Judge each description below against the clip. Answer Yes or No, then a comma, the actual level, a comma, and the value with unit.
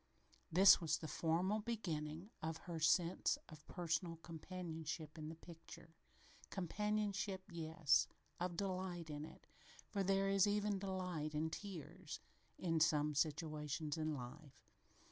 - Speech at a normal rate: No, slow, 125 wpm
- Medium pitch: Yes, medium, 165 Hz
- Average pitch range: Yes, average, 3.4 semitones